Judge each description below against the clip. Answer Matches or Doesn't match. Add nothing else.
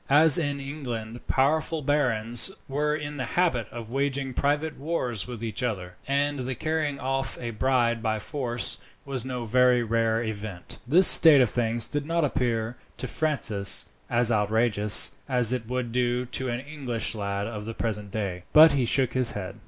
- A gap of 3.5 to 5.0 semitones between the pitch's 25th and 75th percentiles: Matches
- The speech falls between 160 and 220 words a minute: Matches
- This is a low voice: Matches